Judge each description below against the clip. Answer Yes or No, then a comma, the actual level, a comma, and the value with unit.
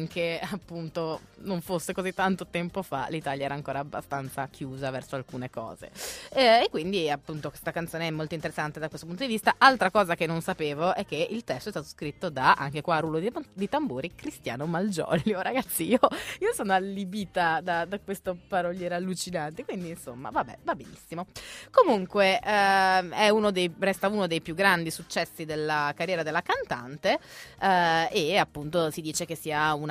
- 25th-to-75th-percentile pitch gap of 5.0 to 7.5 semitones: No, average, 3.8 semitones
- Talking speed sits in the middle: No, fast, 180 wpm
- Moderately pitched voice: Yes, medium, 170 Hz